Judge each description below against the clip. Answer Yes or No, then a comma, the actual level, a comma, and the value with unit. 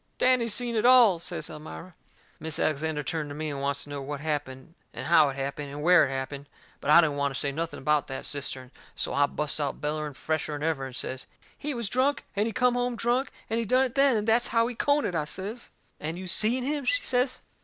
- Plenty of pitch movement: Yes, wide, 8.7 semitones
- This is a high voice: No, medium, 160 Hz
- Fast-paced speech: Yes, fast, 245 wpm